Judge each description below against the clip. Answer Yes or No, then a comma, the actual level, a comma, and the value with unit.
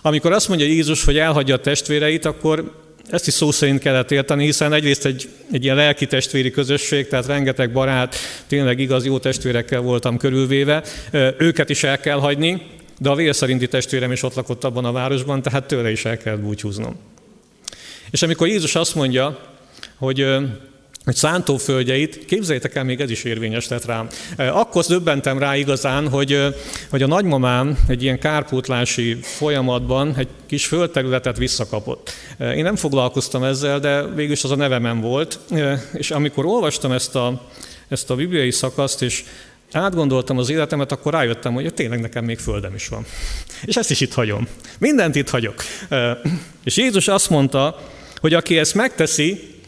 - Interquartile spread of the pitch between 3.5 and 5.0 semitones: No, average, 2.8 semitones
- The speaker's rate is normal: No, fast, 160 wpm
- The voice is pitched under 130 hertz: No, medium, 140 Hz